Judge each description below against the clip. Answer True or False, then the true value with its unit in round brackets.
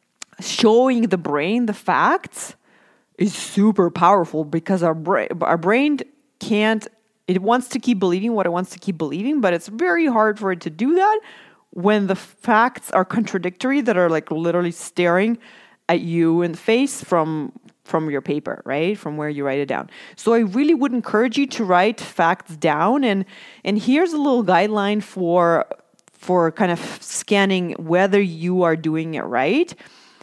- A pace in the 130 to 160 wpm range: False (175 wpm)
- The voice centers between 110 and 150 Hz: False (195 Hz)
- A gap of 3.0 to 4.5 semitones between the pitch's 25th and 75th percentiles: False (5.2 semitones)